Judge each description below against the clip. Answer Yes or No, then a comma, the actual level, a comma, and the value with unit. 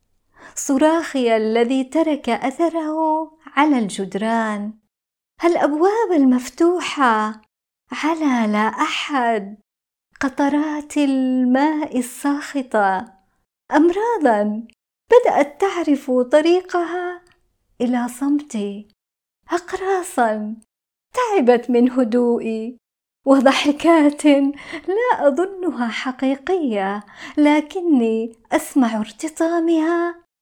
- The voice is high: Yes, very high, 285 Hz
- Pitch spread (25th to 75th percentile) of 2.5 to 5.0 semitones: No, wide, 5.6 semitones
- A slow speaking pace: Yes, slow, 60 wpm